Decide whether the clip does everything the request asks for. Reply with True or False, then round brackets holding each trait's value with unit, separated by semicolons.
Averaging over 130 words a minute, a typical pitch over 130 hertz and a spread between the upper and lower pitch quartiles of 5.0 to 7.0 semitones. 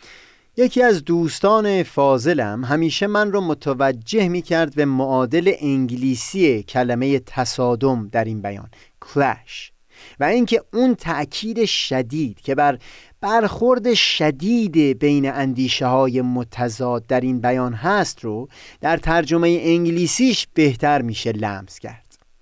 False (120 wpm; 140 Hz; 5.5 semitones)